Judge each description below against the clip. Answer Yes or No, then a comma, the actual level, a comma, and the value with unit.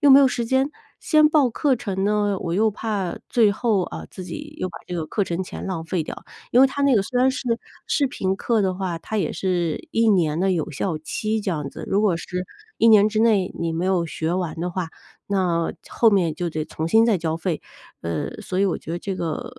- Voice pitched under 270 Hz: Yes, high, 190 Hz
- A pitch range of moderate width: Yes, average, 4.9 semitones